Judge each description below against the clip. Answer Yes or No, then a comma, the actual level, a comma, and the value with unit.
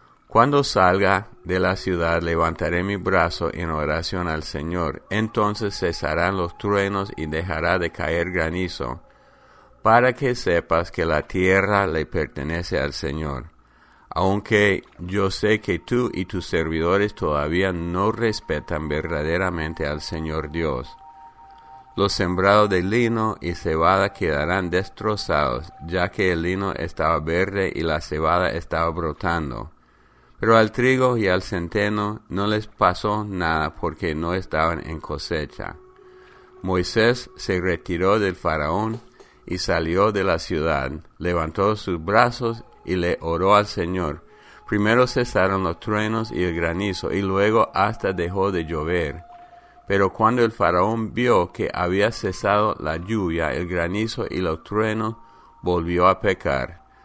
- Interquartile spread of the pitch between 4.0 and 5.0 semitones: Yes, average, 4.4 semitones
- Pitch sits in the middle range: No, very low, 95 Hz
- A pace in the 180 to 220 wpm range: No, slow, 135 wpm